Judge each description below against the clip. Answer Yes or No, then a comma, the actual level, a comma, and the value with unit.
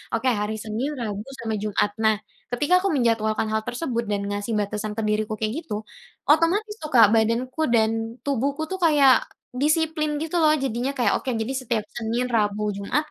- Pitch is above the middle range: Yes, high, 235 Hz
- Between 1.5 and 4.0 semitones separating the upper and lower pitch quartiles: No, average, 5.2 semitones